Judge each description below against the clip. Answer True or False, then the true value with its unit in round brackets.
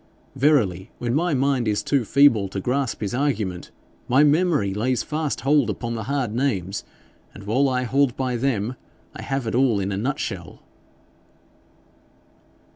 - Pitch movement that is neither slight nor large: True (4.7 semitones)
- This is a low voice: True (125 Hz)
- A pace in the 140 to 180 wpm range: True (155 wpm)